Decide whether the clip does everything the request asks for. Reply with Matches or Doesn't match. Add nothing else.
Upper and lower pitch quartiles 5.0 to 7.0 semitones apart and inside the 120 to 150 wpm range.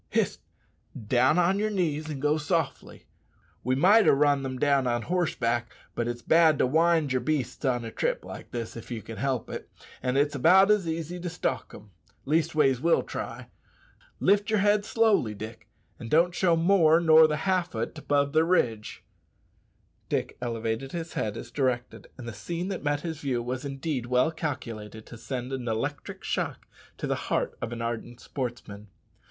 Doesn't match